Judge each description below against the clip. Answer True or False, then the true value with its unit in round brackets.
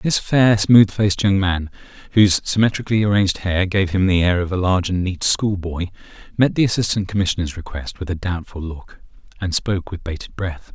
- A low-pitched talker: True (95 Hz)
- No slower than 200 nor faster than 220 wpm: False (190 wpm)